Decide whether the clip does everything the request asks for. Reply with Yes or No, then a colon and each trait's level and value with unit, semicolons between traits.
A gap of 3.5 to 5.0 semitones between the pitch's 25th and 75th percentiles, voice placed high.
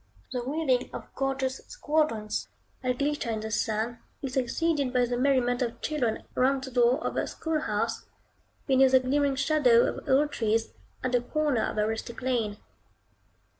No: average, 2.8 semitones; very high, 255 Hz